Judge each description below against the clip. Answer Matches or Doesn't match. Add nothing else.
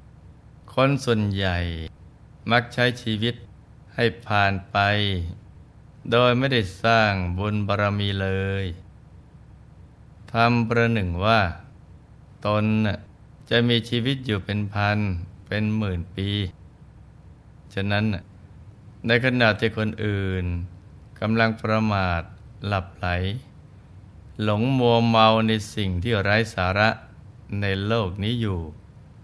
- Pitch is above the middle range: Doesn't match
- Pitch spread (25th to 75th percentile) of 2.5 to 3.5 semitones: Matches